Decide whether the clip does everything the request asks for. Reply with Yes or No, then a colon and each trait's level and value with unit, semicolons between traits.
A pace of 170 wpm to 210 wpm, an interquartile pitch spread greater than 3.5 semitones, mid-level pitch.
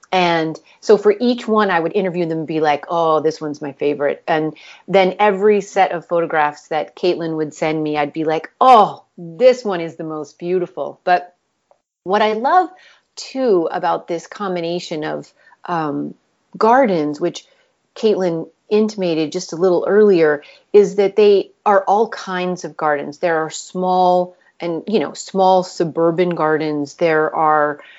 No: average, 160 wpm; average, 4.2 semitones; medium, 175 Hz